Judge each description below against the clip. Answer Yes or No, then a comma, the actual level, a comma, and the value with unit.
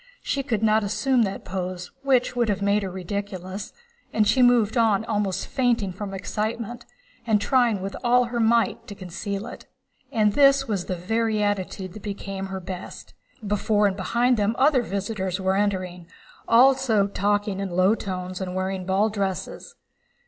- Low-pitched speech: No, high, 205 Hz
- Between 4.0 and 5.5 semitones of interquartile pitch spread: No, average, 3.3 semitones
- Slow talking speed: No, average, 165 wpm